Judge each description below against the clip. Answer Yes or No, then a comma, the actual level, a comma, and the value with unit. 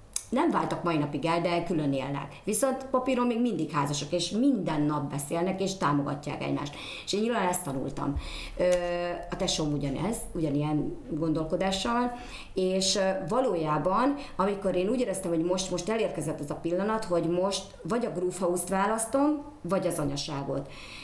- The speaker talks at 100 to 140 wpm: No, average, 150 wpm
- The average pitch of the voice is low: No, medium, 175 Hz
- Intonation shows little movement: No, average, 4.6 semitones